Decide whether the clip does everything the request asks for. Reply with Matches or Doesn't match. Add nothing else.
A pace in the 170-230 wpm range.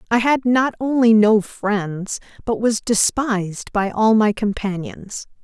Doesn't match